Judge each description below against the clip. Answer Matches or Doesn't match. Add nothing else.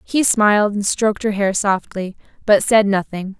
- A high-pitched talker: Matches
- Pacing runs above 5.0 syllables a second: Doesn't match